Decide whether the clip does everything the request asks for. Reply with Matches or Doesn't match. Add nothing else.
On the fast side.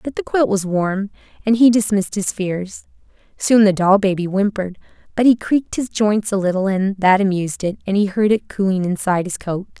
Matches